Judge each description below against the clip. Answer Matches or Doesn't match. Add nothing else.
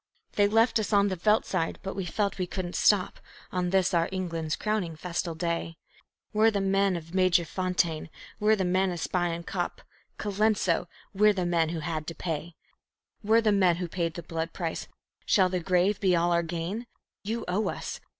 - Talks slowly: Doesn't match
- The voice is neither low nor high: Matches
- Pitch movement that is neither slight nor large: Matches